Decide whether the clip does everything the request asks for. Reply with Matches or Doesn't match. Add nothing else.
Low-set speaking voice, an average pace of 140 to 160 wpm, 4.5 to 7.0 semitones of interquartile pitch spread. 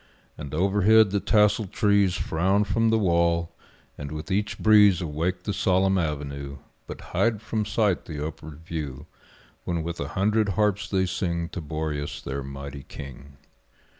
Matches